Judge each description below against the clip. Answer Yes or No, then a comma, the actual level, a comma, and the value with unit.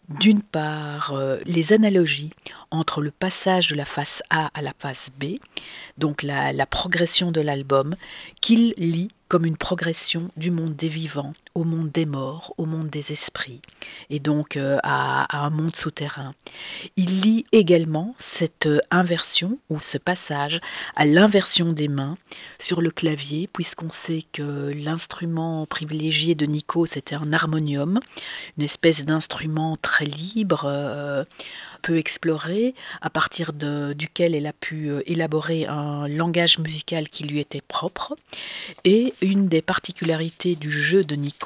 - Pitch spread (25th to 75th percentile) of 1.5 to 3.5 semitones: Yes, average, 2.9 semitones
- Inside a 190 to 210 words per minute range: No, average, 150 wpm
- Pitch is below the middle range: No, medium, 160 Hz